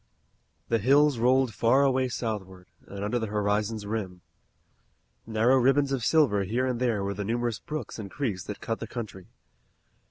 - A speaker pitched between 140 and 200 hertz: No, low, 115 Hz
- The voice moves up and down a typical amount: Yes, average, 3.9 semitones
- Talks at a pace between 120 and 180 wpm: Yes, average, 165 wpm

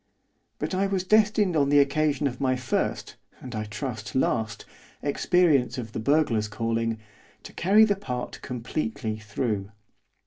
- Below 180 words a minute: Yes, average, 145 wpm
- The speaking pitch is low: Yes, low, 130 Hz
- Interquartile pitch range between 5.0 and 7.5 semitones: Yes, wide, 5.6 semitones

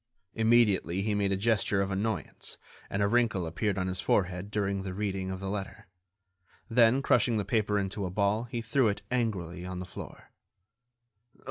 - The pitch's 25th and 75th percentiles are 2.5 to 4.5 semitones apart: Yes, average, 2.8 semitones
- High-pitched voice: No, low, 100 Hz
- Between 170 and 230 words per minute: Yes, average, 175 wpm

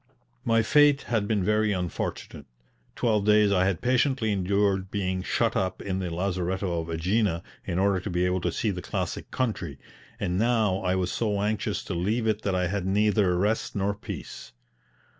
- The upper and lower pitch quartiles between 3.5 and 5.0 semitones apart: No, average, 2.7 semitones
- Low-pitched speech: Yes, low, 100 Hz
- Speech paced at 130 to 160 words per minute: No, average, 180 wpm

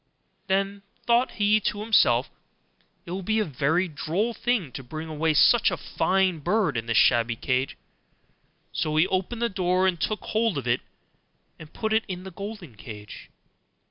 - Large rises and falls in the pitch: Yes, wide, 6.2 semitones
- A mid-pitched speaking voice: Yes, medium, 180 Hz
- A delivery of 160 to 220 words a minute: Yes, average, 175 wpm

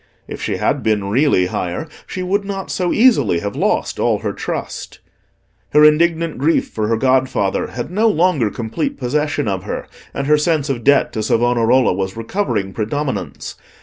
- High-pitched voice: No, low, 130 Hz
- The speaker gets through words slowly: No, average, 170 wpm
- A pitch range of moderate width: No, wide, 6.6 semitones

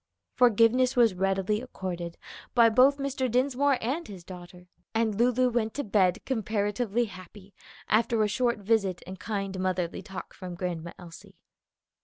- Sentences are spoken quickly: No, average, 145 wpm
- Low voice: No, high, 210 Hz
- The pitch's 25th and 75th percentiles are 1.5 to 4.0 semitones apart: No, average, 4.6 semitones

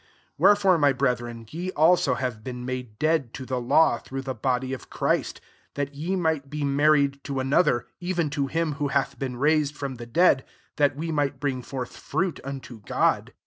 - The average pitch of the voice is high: No, medium, 140 Hz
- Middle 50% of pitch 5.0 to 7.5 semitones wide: No, average, 3.1 semitones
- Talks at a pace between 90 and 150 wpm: No, average, 195 wpm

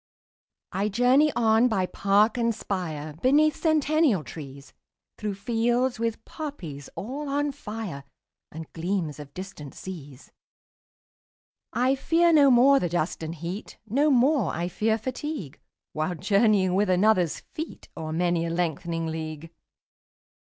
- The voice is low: No, high, 200 Hz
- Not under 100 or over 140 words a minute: Yes, slow, 135 wpm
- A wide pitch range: Yes, wide, 7.3 semitones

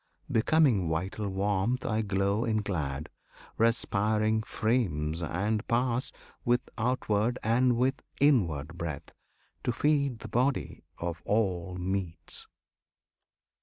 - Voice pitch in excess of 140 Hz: No, low, 110 Hz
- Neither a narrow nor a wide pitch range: Yes, average, 4.7 semitones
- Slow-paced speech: Yes, slow, 105 wpm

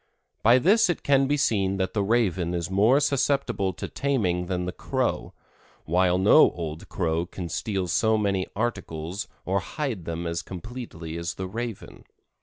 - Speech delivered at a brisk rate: No, average, 165 wpm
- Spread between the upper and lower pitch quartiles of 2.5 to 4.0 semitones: No, average, 5.3 semitones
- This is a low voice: Yes, very low, 95 Hz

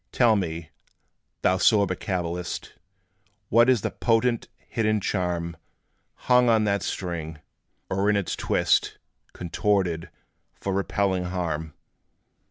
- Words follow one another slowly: Yes, slow, 110 wpm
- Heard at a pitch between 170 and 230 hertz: No, very low, 95 Hz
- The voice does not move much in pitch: No, average, 3.7 semitones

